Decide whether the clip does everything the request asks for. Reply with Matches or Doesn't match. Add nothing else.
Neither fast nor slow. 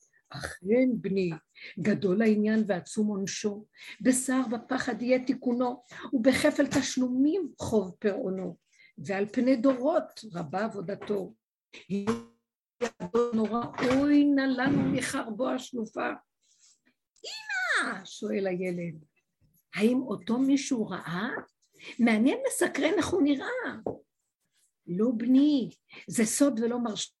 Doesn't match